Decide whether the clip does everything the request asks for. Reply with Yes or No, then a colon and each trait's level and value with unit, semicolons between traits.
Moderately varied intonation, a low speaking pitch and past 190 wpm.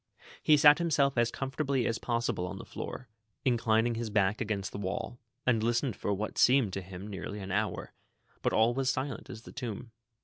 Yes: average, 3.9 semitones; low, 115 Hz; average, 200 wpm